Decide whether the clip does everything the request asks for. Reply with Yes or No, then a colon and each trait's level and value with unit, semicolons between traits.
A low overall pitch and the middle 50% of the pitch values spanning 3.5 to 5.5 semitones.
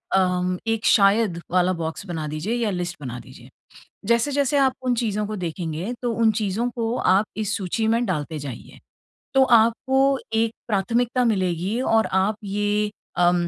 No: high, 210 Hz; average, 4.5 semitones